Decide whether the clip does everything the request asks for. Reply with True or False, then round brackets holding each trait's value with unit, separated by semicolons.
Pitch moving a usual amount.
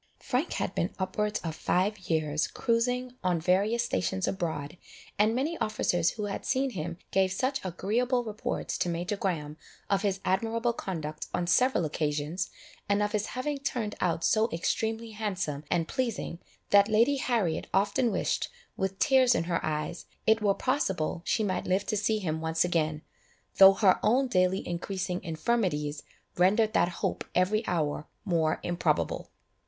True (4.8 semitones)